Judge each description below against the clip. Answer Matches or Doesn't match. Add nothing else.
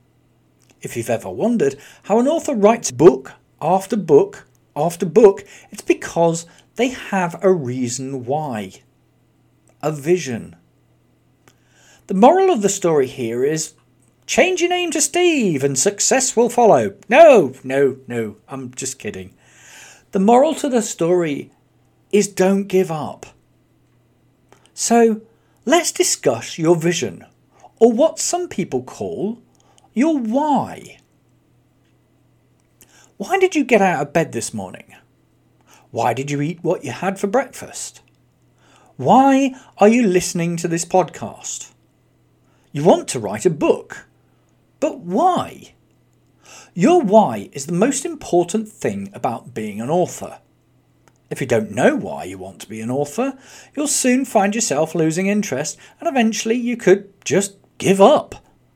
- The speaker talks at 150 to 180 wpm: Doesn't match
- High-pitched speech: Matches